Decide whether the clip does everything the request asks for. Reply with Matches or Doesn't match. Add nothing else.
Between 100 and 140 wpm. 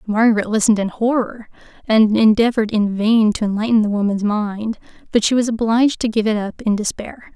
Doesn't match